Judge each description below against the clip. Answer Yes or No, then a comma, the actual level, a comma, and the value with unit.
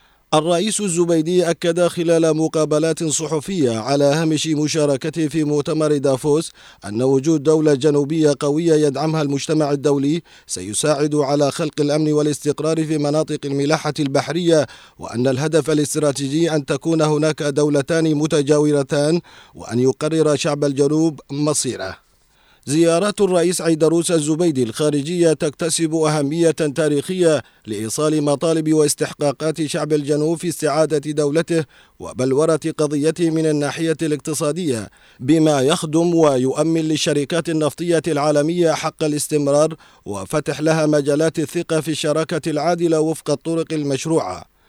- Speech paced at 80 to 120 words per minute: Yes, average, 110 wpm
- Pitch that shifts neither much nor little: No, narrow, 1.6 semitones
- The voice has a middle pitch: Yes, medium, 155 Hz